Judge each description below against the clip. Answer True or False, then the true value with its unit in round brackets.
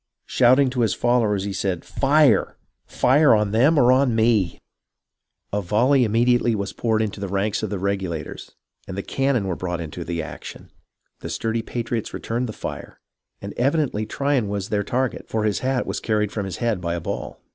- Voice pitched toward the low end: True (110 Hz)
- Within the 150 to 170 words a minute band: False (195 wpm)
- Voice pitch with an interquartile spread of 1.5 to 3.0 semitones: False (3.9 semitones)